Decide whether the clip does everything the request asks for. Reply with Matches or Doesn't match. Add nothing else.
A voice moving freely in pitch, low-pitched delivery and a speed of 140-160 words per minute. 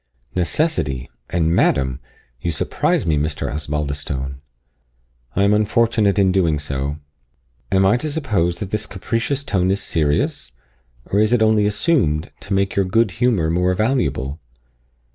Matches